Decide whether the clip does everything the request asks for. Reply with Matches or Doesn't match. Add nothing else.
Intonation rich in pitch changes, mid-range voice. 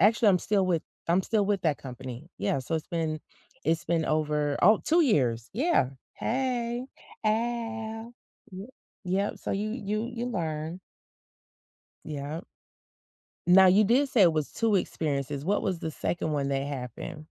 Matches